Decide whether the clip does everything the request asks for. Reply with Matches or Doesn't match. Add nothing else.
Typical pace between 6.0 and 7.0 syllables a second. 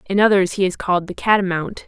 Matches